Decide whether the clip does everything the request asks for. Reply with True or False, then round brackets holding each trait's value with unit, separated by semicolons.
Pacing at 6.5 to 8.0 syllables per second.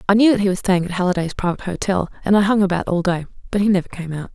True (7.4 syllables/s)